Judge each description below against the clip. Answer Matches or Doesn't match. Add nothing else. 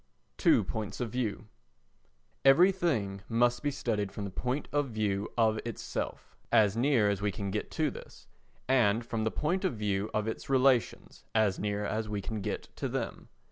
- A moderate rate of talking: Matches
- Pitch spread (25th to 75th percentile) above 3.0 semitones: Matches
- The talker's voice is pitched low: Matches